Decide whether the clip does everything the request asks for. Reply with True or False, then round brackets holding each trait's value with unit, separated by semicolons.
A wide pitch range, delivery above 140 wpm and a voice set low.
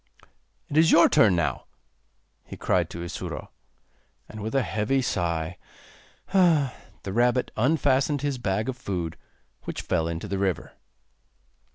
False (7.1 semitones; 135 wpm; 110 Hz)